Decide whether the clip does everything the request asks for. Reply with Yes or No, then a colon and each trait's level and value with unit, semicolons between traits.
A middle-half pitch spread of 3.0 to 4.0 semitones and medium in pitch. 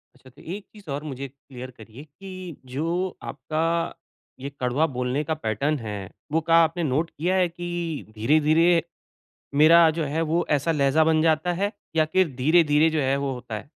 Yes: average, 3.7 semitones; medium, 155 Hz